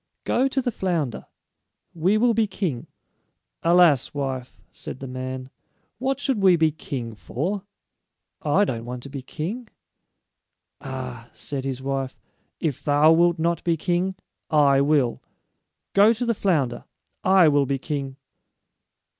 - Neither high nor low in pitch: Yes, medium, 150 Hz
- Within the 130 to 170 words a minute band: Yes, average, 140 wpm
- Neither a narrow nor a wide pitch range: No, wide, 6.1 semitones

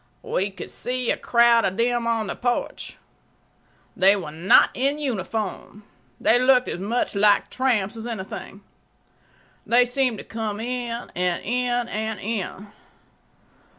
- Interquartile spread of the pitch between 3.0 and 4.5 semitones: Yes, average, 3.4 semitones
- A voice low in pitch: No, high, 230 Hz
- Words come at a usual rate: No, slow, 130 wpm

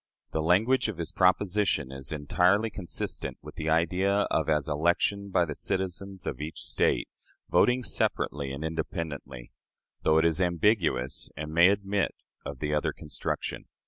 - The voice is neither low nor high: No, very low, 85 Hz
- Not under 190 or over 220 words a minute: No, average, 150 wpm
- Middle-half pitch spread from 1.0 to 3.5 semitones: No, average, 4.4 semitones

